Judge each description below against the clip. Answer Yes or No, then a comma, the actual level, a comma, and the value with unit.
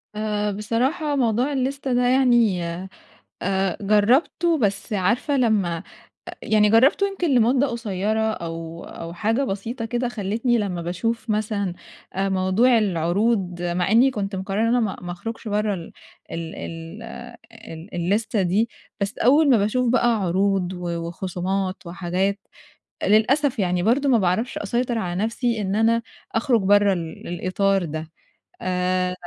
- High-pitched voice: Yes, high, 205 Hz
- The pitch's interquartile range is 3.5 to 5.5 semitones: Yes, average, 4.5 semitones